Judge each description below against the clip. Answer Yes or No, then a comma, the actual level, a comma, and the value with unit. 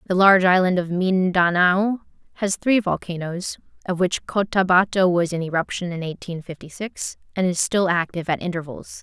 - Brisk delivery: No, average, 160 wpm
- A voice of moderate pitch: Yes, medium, 180 Hz